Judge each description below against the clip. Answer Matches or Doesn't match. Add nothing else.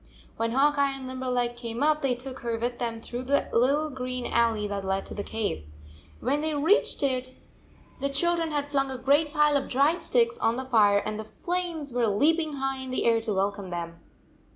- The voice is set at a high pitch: Matches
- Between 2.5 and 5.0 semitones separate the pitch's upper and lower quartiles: Matches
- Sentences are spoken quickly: Matches